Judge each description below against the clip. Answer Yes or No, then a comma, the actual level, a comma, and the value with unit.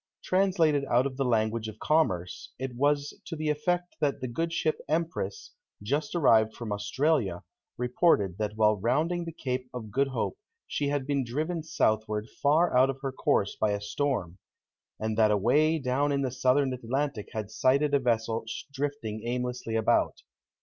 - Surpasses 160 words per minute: Yes, average, 170 wpm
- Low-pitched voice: Yes, low, 130 Hz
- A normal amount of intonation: Yes, average, 4.9 semitones